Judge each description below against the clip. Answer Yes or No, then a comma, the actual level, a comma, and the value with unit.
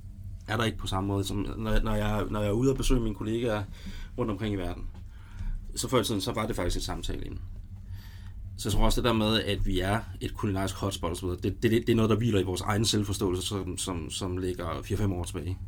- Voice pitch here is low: Yes, low, 100 Hz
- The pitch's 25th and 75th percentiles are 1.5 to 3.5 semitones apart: Yes, narrow, 2.4 semitones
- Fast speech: Yes, fast, 250 wpm